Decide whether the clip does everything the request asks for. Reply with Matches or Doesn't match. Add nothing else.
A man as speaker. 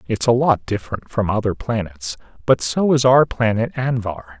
Matches